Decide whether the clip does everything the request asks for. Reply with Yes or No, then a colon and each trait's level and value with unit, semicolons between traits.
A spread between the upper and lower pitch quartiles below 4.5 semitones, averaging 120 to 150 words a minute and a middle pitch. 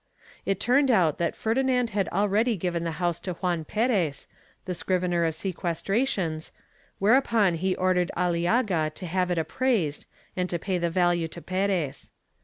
No: average, 3.3 semitones; average, 160 wpm; medium, 180 Hz